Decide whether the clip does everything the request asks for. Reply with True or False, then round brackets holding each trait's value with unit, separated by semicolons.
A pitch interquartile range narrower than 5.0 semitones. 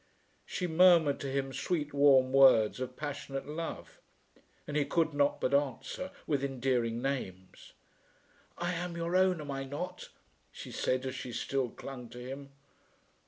True (3.4 semitones)